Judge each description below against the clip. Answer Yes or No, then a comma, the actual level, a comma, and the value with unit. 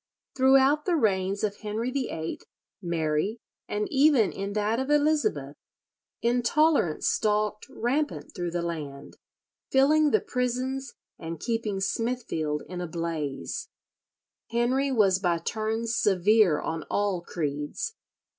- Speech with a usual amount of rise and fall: No, wide, 7.3 semitones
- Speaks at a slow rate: Yes, slow, 115 wpm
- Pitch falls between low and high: No, high, 215 Hz